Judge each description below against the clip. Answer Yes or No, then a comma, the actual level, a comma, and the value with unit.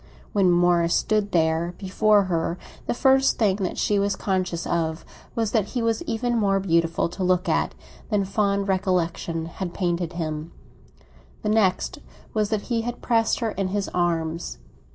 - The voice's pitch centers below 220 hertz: Yes, high, 190 Hz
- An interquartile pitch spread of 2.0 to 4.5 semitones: Yes, average, 3.8 semitones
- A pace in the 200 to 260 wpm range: No, average, 165 wpm